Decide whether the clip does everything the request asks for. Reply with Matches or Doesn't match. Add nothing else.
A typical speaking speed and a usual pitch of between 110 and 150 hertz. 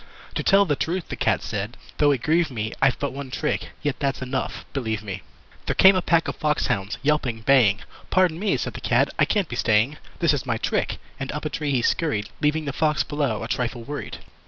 Doesn't match